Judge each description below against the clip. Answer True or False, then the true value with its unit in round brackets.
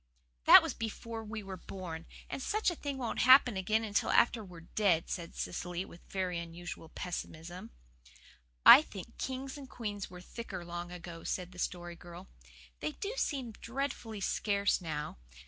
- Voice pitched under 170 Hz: False (190 Hz)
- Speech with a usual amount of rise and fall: True (4.9 semitones)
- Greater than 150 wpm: True (165 wpm)